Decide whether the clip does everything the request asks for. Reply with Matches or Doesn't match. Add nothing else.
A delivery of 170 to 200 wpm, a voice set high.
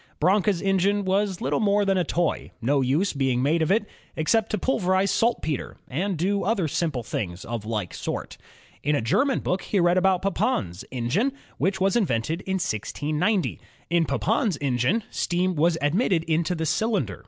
Doesn't match